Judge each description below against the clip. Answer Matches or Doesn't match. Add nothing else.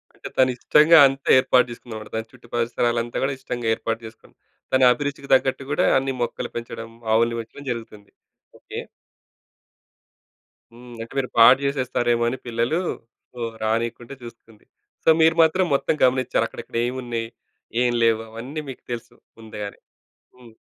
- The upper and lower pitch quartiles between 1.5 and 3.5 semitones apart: Matches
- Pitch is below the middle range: Matches